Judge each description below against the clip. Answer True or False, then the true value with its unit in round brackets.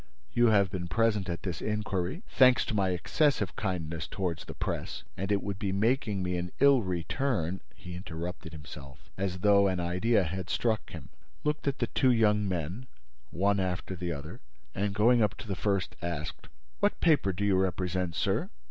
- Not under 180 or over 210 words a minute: True (185 wpm)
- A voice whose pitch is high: False (95 Hz)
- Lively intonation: False (3.3 semitones)